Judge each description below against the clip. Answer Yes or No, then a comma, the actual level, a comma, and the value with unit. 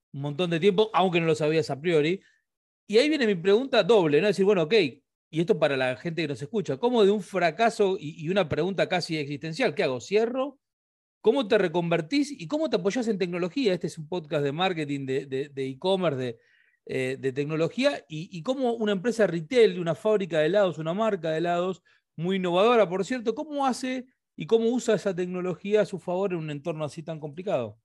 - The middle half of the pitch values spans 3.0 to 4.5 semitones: No, wide, 5.4 semitones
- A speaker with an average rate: No, fast, 215 wpm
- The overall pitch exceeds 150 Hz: Yes, medium, 185 Hz